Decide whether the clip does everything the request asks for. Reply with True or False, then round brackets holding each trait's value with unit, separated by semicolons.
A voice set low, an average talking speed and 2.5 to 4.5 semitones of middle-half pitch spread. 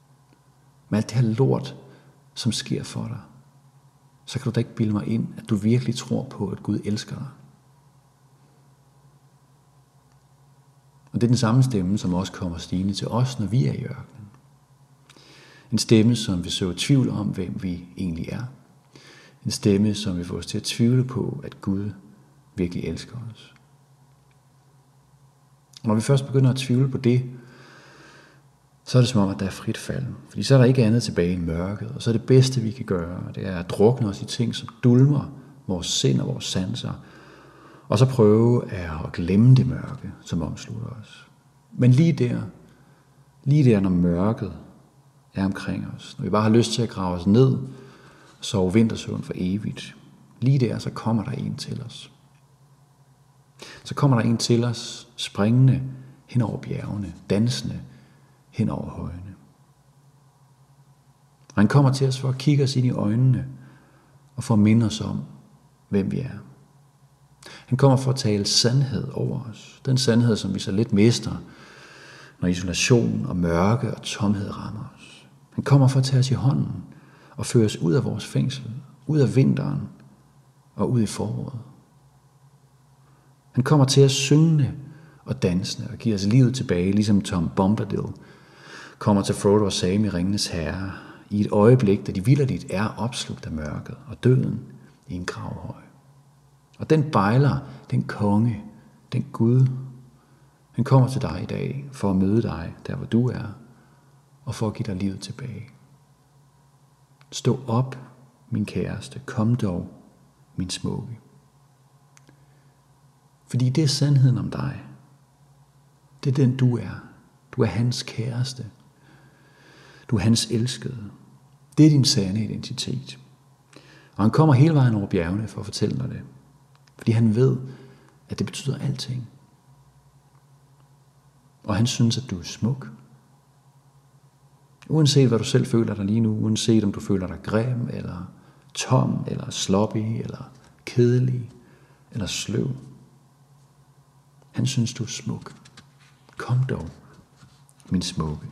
True (130 Hz; 160 wpm; 4.2 semitones)